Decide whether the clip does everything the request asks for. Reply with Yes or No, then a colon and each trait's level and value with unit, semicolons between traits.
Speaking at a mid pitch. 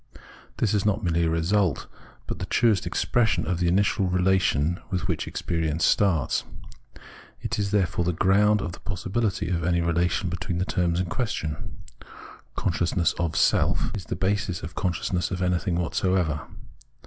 No: very low, 90 Hz